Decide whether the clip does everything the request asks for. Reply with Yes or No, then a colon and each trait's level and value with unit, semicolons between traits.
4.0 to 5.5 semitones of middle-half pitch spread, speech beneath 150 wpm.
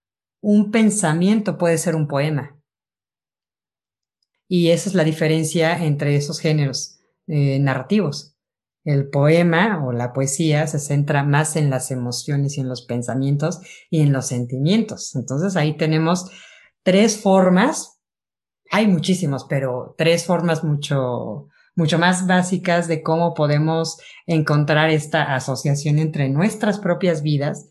No: average, 3.5 semitones; average, 130 wpm